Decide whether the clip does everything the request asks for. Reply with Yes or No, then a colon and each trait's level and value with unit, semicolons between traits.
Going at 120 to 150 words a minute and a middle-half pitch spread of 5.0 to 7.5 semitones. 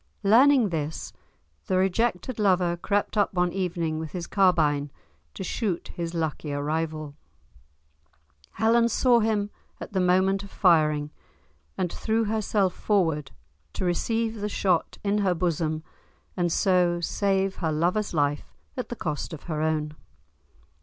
No: average, 140 wpm; average, 4.3 semitones